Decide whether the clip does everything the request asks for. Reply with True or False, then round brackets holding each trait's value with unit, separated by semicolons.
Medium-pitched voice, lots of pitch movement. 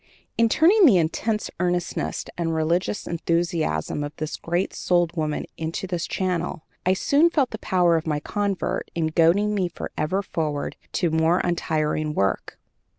False (170 Hz; 3.0 semitones)